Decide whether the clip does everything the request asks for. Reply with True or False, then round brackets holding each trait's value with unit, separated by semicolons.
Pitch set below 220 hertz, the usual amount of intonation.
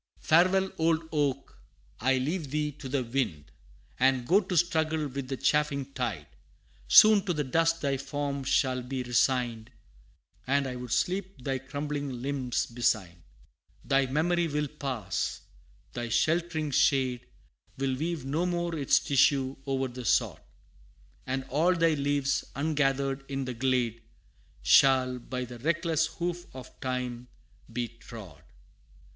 True (135 Hz; 3.6 semitones)